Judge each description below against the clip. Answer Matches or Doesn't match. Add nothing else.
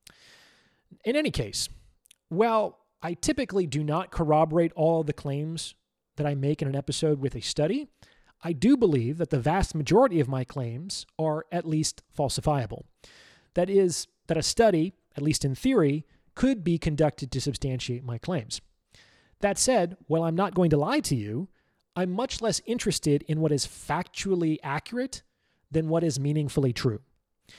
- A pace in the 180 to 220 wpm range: Doesn't match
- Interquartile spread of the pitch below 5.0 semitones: Matches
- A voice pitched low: Doesn't match